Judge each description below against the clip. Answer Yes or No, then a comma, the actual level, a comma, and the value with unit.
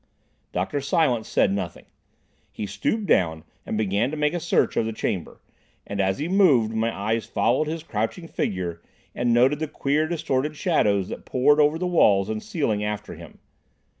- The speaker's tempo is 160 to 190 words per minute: Yes, average, 175 wpm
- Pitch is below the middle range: Yes, low, 120 Hz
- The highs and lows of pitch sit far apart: Yes, wide, 6.8 semitones